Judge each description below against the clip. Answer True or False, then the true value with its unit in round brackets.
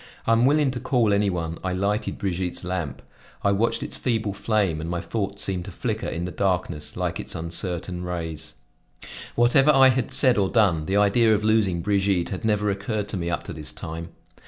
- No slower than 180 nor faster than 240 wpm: True (195 wpm)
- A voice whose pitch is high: False (100 Hz)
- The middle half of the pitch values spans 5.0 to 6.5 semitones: False (4.0 semitones)